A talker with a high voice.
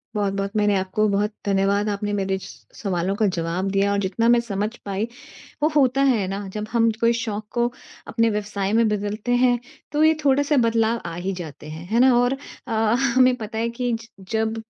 Yes: high, 210 Hz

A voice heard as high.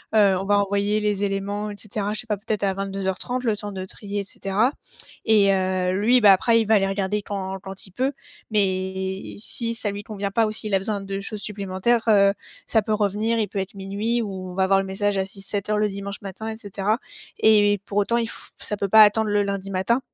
Yes: high, 200 Hz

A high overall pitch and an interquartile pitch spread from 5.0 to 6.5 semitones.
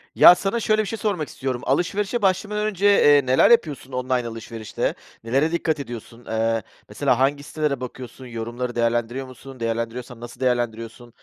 No: low, 130 Hz; wide, 5.4 semitones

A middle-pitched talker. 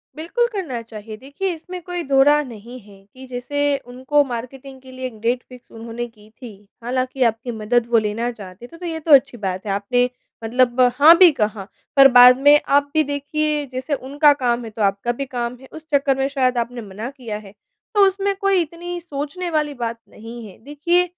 No: very high, 260 Hz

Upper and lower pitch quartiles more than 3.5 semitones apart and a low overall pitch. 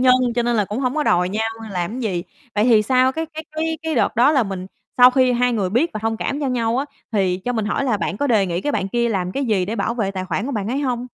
No: average, 4.3 semitones; high, 235 Hz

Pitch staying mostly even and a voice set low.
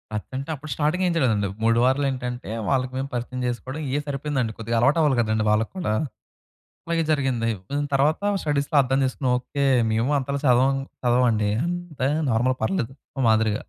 No: average, 3.4 semitones; low, 130 Hz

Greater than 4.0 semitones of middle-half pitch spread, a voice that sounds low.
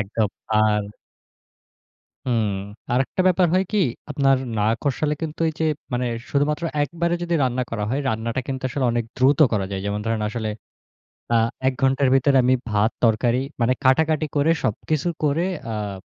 Yes: average, 5.0 semitones; low, 130 Hz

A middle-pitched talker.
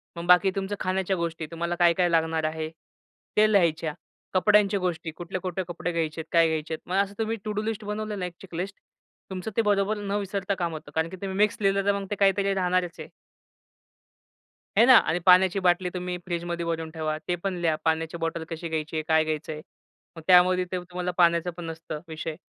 Yes: medium, 180 Hz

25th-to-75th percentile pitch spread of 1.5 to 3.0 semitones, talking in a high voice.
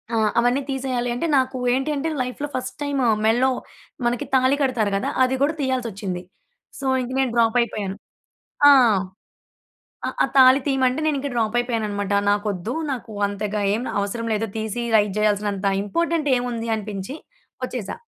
No: average, 3.8 semitones; high, 240 Hz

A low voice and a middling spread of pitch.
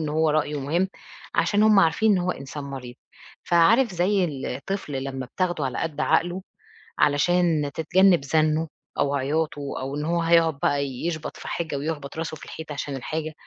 No: medium, 155 Hz; average, 3.5 semitones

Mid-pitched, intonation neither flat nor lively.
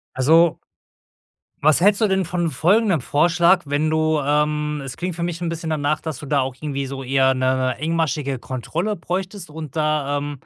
Yes: medium, 155 Hz; average, 3.5 semitones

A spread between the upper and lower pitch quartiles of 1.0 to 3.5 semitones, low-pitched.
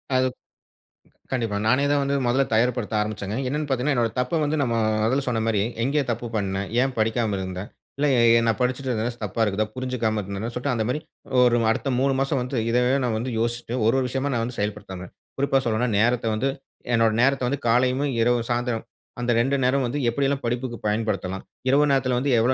Yes: average, 3.1 semitones; low, 120 Hz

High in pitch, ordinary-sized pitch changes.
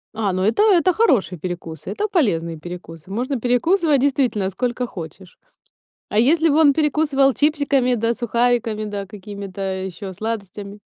No: high, 230 Hz; wide, 6.6 semitones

